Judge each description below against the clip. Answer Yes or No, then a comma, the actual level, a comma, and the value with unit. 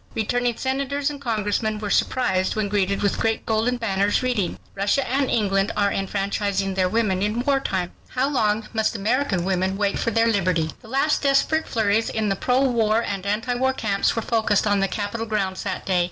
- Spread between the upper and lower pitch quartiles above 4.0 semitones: No, average, 3.6 semitones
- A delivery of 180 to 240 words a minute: Yes, average, 195 wpm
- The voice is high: Yes, high, 215 Hz